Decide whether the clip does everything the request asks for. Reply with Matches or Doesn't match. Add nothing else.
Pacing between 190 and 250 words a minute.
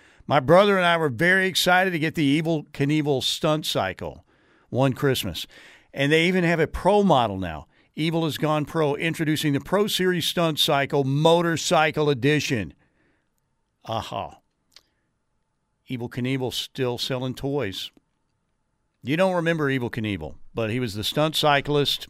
Doesn't match